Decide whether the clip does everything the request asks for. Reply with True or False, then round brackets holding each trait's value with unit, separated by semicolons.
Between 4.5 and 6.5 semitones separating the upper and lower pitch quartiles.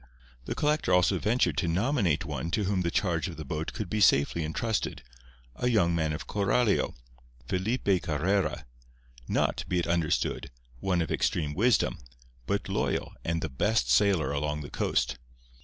True (5.2 semitones)